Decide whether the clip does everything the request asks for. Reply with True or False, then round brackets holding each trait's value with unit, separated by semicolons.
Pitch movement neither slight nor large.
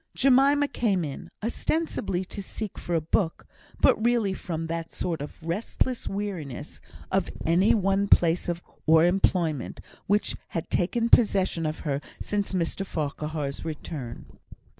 True (4.3 semitones)